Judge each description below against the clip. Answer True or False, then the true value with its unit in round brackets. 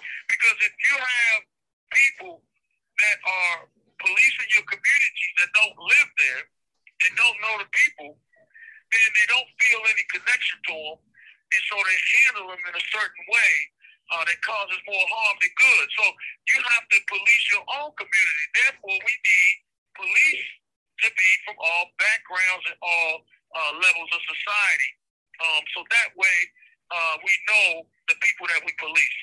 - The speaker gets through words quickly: False (160 wpm)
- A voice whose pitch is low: False (205 Hz)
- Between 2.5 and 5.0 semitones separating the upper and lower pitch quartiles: False (5.5 semitones)